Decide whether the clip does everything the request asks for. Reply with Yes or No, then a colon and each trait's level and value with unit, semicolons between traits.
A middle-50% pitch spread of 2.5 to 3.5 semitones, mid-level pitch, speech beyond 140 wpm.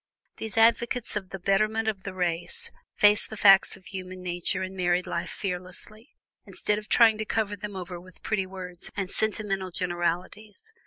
No: average, 2.8 semitones; high, 195 Hz; average, 170 wpm